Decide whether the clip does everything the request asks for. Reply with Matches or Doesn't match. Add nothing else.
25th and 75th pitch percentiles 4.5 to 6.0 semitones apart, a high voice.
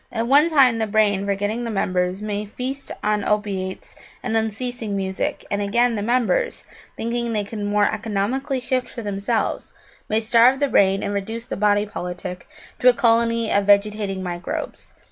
Doesn't match